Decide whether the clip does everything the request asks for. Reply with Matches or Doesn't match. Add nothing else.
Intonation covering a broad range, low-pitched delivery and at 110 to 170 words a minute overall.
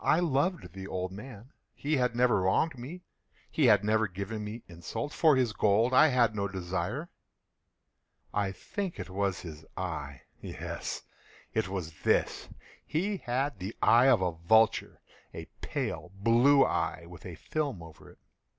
Matches